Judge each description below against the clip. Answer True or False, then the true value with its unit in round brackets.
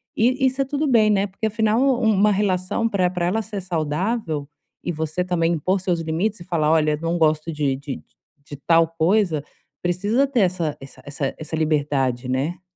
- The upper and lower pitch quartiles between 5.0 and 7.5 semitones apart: True (5.4 semitones)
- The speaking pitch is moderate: True (175 Hz)